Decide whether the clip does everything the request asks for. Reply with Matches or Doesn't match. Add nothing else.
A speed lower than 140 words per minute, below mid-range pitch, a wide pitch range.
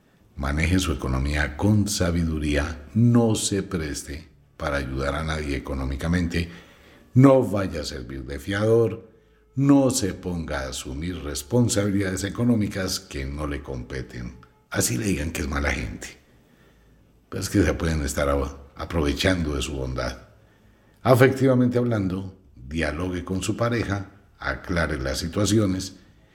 Matches